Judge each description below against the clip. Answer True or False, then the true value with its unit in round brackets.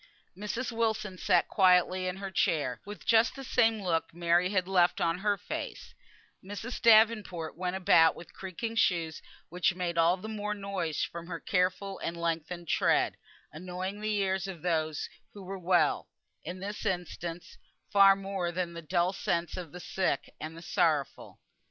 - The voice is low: False (185 Hz)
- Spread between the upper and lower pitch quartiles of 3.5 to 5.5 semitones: False (2.8 semitones)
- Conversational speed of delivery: True (165 wpm)